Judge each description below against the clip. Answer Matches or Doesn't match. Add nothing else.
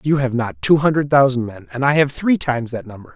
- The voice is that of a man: Matches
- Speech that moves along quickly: Matches